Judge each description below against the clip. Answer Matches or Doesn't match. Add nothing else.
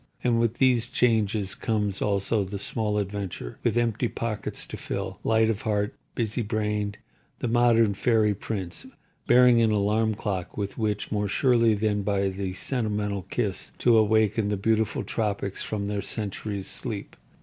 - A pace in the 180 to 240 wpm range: Doesn't match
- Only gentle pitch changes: Matches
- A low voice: Matches